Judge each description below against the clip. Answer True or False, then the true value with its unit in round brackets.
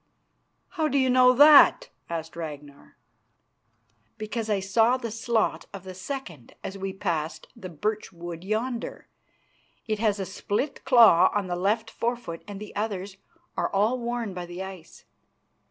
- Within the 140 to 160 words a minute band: True (155 wpm)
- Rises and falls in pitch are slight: False (4.3 semitones)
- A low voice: False (205 Hz)